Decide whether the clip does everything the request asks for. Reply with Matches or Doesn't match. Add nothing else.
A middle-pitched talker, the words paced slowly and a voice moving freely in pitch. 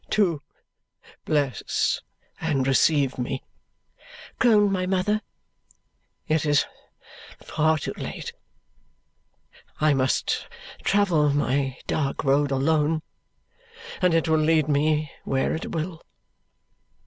Doesn't match